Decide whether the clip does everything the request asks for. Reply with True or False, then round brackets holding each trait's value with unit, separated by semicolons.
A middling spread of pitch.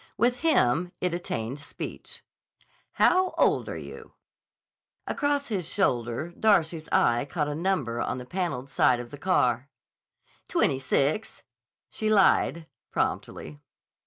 False (7.4 semitones)